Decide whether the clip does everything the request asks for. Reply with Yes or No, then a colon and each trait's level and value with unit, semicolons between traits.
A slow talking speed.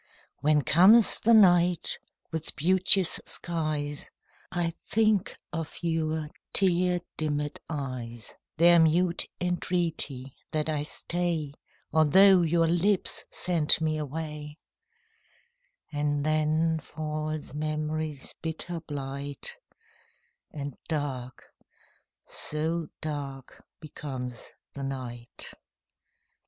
Yes: slow, 90 wpm